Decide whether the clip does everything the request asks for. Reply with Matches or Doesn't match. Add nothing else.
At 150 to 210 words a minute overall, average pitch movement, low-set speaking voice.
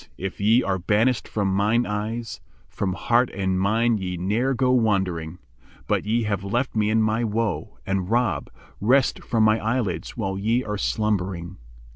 Matches